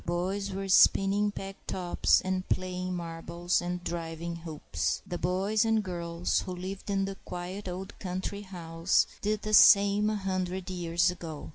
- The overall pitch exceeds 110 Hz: Yes, medium, 185 Hz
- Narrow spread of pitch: Yes, narrow, 2.1 semitones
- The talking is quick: No, average, 155 wpm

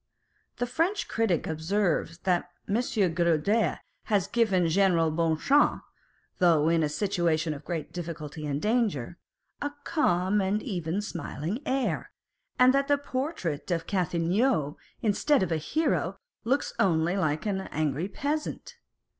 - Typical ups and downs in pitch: No, wide, 5.8 semitones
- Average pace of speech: No, slow, 130 wpm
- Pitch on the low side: No, medium, 180 Hz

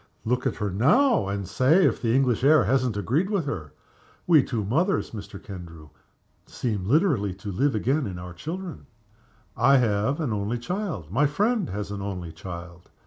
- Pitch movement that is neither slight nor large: No, wide, 7.1 semitones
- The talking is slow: No, average, 175 wpm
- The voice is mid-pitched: No, low, 115 Hz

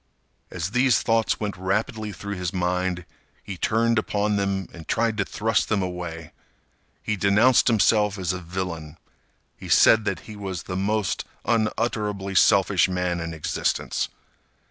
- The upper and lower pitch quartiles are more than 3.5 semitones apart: No, average, 3.1 semitones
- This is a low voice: Yes, low, 100 Hz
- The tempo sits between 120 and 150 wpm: Yes, average, 145 wpm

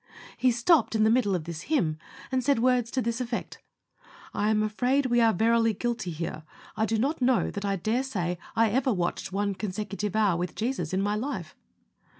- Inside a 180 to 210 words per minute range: Yes, average, 200 wpm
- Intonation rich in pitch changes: No, average, 4.1 semitones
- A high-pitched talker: Yes, high, 220 Hz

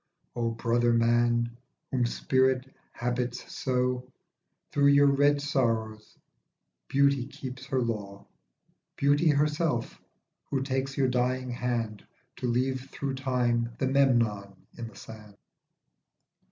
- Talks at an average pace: No, slow, 115 wpm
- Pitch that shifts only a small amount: Yes, narrow, 2.3 semitones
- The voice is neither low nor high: No, low, 125 Hz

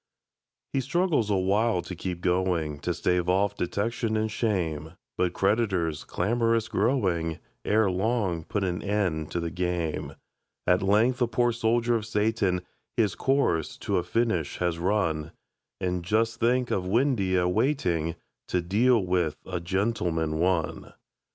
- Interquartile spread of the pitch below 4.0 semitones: No, average, 4.5 semitones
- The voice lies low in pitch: Yes, very low, 95 Hz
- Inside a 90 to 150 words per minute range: Yes, average, 140 wpm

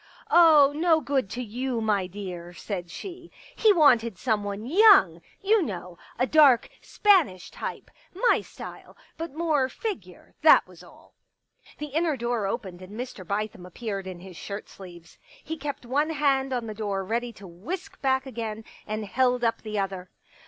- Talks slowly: No, average, 175 wpm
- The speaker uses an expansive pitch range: Yes, wide, 7.0 semitones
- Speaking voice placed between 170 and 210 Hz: No, high, 235 Hz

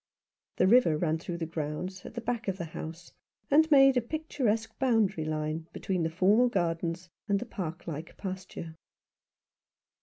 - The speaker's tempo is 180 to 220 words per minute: No, average, 160 wpm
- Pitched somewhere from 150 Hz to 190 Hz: Yes, medium, 185 Hz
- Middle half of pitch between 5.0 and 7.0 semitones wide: Yes, wide, 5.6 semitones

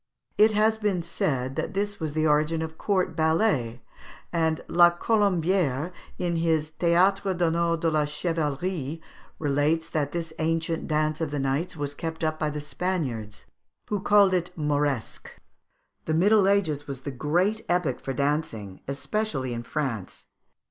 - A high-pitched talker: No, medium, 160 Hz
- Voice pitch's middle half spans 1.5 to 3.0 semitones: No, average, 3.7 semitones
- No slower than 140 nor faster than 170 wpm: Yes, average, 155 wpm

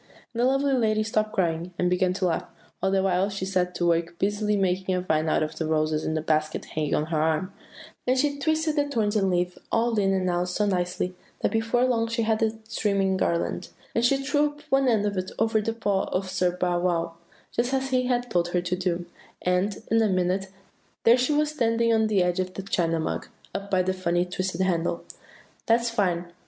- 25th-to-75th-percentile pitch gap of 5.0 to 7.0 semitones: No, average, 4.2 semitones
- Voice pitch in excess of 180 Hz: Yes, high, 190 Hz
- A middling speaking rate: No, fast, 225 wpm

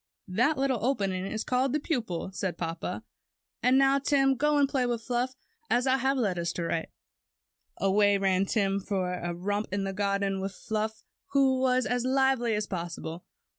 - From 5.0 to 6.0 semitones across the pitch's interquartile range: Yes, wide, 5.4 semitones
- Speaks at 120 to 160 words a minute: No, average, 175 wpm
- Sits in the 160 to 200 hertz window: No, high, 220 Hz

